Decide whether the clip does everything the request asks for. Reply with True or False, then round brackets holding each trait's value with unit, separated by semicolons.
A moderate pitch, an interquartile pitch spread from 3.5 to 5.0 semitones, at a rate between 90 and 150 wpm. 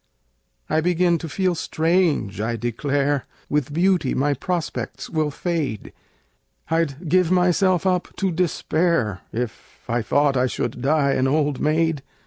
True (155 Hz; 4.6 semitones; 135 wpm)